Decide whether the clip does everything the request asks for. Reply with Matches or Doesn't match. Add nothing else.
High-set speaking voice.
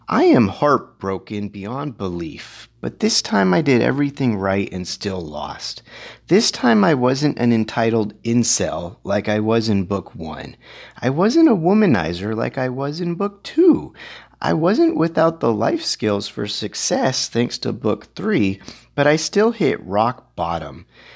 Doesn't match